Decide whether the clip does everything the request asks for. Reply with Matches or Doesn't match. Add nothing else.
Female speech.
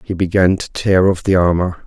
Doesn't match